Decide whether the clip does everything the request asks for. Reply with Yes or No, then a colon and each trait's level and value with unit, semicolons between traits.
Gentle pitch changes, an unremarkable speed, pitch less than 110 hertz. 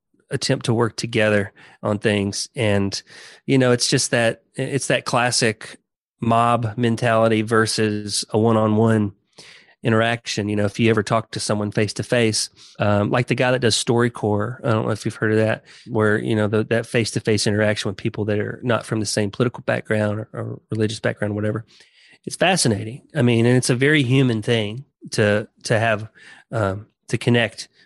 No: narrow, 2.1 semitones; average, 190 wpm; low, 115 Hz